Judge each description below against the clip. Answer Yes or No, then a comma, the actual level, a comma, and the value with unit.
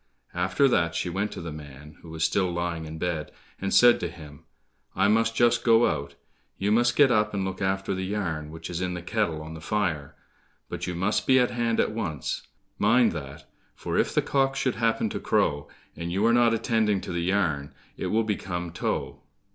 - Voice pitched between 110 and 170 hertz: No, very low, 95 Hz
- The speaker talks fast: Yes, fast, 210 wpm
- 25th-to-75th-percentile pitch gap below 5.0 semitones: No, wide, 5.5 semitones